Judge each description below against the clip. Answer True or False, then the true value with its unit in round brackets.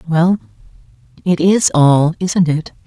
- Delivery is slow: True (125 wpm)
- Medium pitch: True (160 Hz)